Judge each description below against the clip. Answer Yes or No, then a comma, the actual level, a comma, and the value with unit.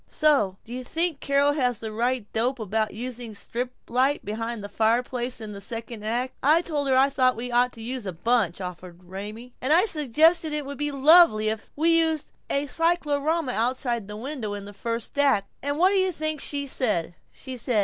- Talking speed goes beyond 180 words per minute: Yes, average, 200 wpm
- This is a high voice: Yes, very high, 250 Hz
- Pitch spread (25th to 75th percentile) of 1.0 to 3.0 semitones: No, average, 4.7 semitones